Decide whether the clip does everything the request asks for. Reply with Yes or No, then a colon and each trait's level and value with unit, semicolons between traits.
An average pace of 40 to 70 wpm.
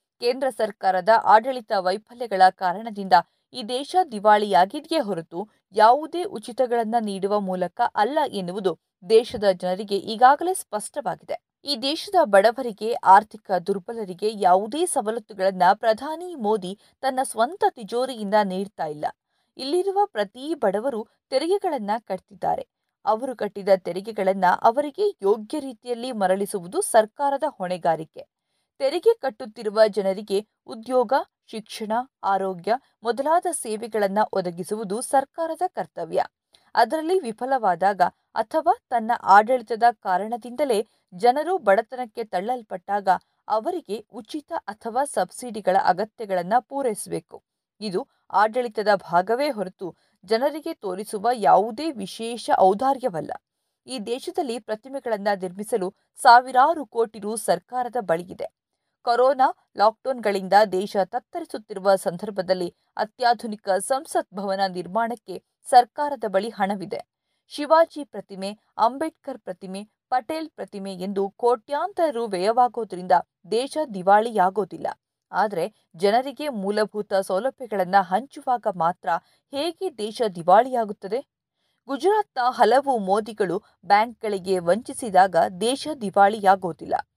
No: average, 90 wpm